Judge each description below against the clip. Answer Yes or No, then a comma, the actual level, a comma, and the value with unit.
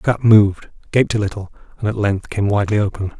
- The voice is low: Yes, low, 105 Hz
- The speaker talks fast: Yes, fast, 225 wpm